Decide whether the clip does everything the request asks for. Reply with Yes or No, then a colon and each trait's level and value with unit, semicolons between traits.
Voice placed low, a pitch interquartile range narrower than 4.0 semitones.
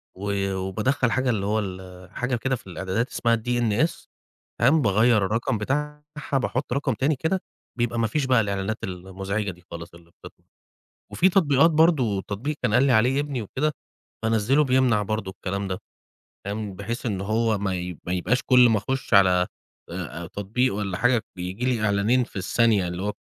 No: low, 110 Hz; average, 4.8 semitones